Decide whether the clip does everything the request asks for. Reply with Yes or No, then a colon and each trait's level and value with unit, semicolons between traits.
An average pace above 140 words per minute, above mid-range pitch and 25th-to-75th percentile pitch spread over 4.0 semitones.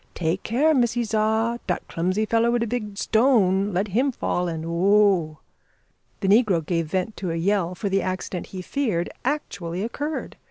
Yes: average, 170 wpm; high, 200 Hz; average, 4.5 semitones